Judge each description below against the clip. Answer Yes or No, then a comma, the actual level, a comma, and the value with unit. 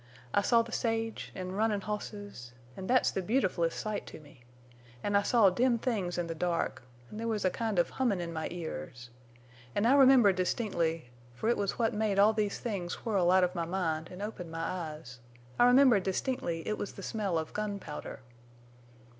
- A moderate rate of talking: Yes, average, 180 wpm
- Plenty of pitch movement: No, average, 4.9 semitones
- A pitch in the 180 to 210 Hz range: Yes, high, 190 Hz